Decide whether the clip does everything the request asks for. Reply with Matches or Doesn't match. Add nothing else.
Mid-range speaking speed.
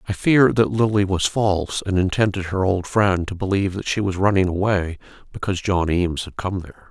Doesn't match